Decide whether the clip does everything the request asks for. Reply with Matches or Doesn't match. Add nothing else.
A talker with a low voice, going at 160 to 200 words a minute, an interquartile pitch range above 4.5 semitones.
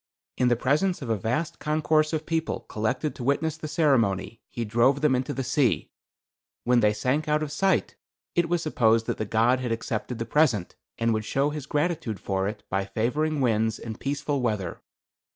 Matches